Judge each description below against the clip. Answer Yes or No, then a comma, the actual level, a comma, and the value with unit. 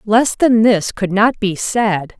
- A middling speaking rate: Yes, average, 190 wpm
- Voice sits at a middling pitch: No, high, 210 Hz